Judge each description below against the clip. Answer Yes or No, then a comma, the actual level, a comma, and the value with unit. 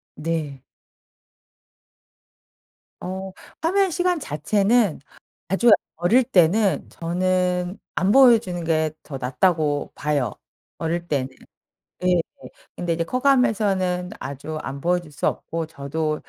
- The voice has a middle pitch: Yes, medium, 175 Hz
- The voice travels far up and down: No, average, 4.5 semitones